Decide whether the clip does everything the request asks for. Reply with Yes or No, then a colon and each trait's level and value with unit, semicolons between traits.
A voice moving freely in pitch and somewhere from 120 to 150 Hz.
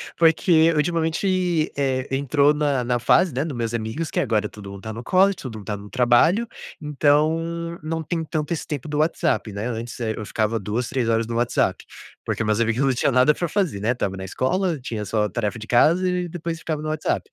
Yes: wide, 6.1 semitones; medium, 140 Hz